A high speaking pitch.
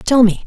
Yes: high, 230 Hz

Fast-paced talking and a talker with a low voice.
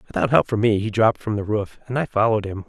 Yes: fast, 290 wpm; low, 105 Hz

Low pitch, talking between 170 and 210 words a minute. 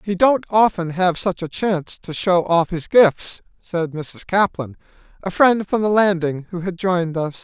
No: medium, 180 Hz; average, 195 wpm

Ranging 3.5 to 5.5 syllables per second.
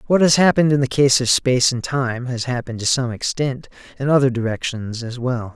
No: 5.7 syllables/s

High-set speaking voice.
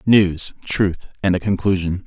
No: very low, 95 Hz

